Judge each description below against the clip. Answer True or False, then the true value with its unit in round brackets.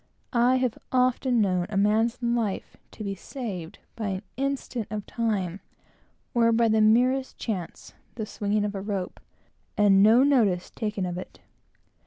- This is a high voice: True (215 Hz)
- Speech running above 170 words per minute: False (155 wpm)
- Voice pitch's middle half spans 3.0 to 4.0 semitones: True (3.4 semitones)